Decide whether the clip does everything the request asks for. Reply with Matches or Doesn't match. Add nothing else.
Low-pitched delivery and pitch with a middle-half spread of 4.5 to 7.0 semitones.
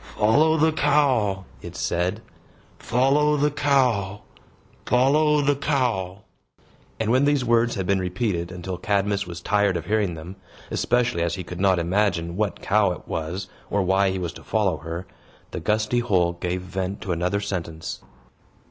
Matches